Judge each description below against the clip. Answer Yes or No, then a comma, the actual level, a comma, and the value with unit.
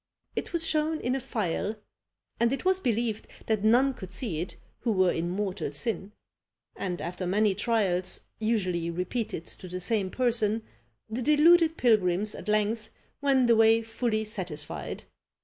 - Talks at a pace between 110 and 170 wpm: Yes, average, 150 wpm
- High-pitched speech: Yes, high, 215 Hz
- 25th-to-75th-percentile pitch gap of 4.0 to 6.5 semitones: Yes, average, 4.6 semitones